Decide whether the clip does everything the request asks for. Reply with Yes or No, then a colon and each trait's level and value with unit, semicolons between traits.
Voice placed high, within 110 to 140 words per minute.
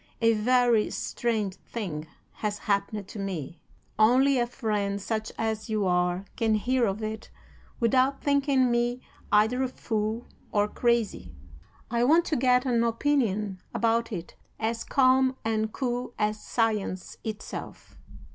Yes: high, 225 Hz; slow, 135 wpm